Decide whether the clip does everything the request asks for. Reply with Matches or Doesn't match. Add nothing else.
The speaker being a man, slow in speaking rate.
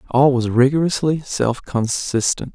Matches